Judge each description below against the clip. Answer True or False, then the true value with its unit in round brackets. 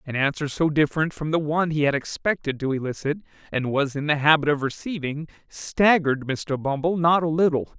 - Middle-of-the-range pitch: True (150 Hz)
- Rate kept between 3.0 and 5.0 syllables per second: False (5.6 syllables/s)